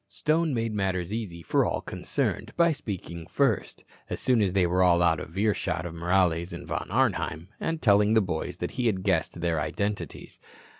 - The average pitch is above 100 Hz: No, very low, 95 Hz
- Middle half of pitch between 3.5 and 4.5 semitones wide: Yes, average, 4.2 semitones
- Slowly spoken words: No, average, 185 wpm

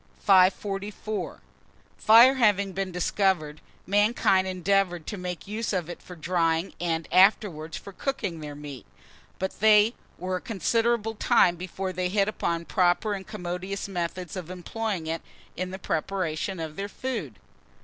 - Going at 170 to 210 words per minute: No, average, 145 wpm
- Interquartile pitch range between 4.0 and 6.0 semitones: No, average, 2.9 semitones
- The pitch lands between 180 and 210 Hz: Yes, medium, 185 Hz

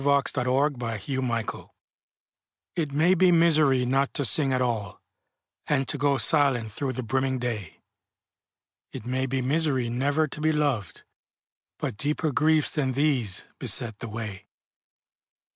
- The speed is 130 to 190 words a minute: Yes, average, 145 wpm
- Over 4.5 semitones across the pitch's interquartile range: No, average, 3.7 semitones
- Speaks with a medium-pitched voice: No, low, 130 Hz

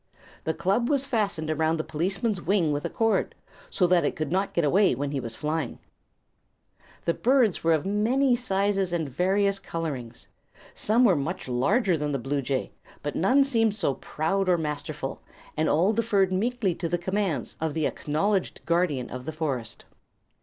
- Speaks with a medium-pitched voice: Yes, medium, 175 Hz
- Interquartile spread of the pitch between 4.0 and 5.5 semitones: Yes, average, 5.1 semitones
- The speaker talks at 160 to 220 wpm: Yes, average, 175 wpm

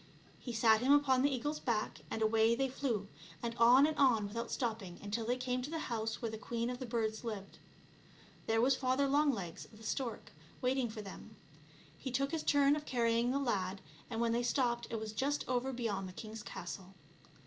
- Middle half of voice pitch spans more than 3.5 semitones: No, average, 3.2 semitones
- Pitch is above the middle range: Yes, high, 235 Hz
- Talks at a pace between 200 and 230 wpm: Yes, fast, 205 wpm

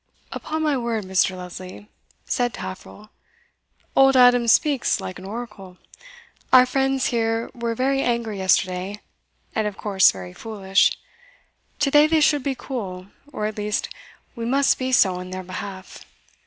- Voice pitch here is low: No, high, 225 Hz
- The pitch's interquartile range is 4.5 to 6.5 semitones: Yes, average, 5.3 semitones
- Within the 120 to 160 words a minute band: Yes, average, 145 wpm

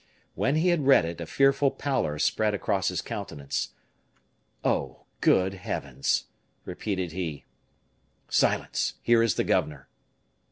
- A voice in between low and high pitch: No, very low, 95 Hz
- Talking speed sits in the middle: No, slow, 125 wpm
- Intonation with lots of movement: Yes, wide, 8.4 semitones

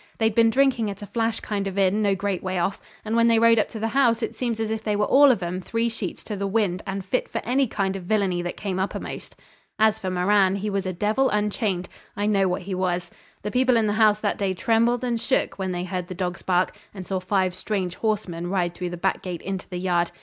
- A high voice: Yes, high, 200 Hz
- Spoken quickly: Yes, fast, 250 wpm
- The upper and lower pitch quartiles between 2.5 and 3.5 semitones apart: Yes, average, 3.2 semitones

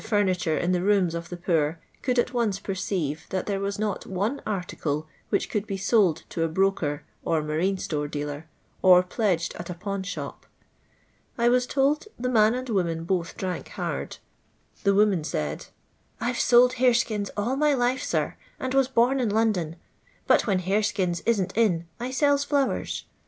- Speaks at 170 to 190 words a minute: Yes, average, 180 wpm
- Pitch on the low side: No, high, 200 Hz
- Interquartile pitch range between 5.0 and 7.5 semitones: Yes, wide, 5.5 semitones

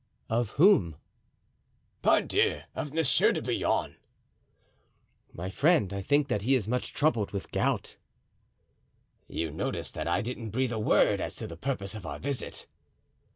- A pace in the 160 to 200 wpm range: No, average, 150 wpm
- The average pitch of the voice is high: No, low, 115 Hz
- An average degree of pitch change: No, wide, 5.8 semitones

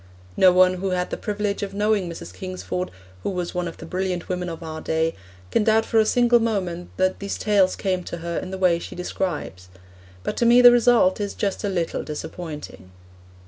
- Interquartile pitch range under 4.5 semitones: Yes, average, 3.4 semitones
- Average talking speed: No, fast, 210 wpm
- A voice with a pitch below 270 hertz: Yes, medium, 185 Hz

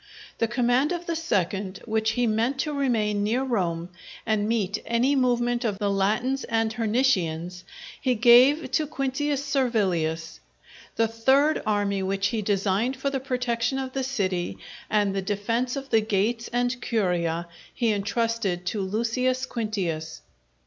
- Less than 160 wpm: Yes, average, 150 wpm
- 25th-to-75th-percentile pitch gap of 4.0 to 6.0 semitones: Yes, average, 4.4 semitones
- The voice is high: Yes, high, 225 Hz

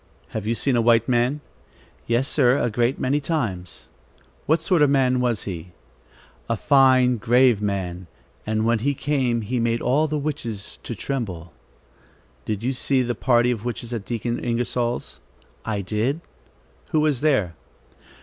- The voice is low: Yes, low, 120 Hz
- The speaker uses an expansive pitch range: No, average, 3.5 semitones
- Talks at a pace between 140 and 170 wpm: Yes, average, 160 wpm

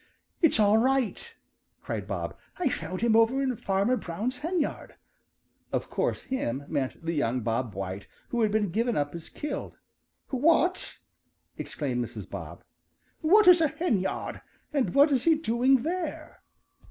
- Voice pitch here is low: No, high, 235 Hz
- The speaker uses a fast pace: No, average, 150 wpm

